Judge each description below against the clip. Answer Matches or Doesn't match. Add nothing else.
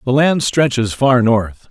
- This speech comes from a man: Matches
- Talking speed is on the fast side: Doesn't match